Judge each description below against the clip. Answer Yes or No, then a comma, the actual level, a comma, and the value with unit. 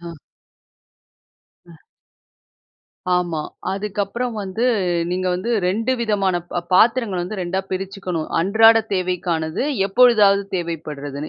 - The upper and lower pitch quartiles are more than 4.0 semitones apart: No, average, 3.4 semitones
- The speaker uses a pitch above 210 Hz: No, high, 190 Hz